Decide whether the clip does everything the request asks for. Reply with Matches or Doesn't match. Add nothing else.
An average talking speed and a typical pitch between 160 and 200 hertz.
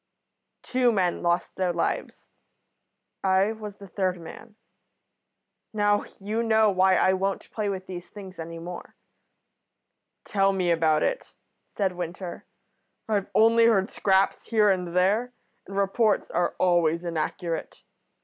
Doesn't match